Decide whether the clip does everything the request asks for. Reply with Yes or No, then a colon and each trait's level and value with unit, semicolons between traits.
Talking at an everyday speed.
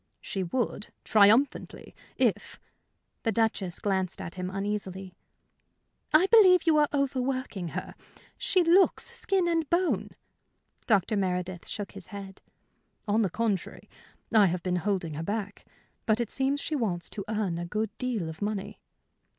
Yes: average, 150 wpm